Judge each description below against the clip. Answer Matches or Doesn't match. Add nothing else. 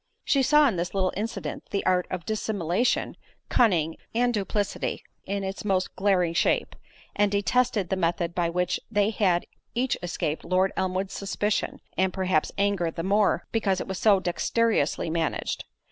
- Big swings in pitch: Doesn't match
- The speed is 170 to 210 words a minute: Doesn't match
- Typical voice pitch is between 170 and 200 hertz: Matches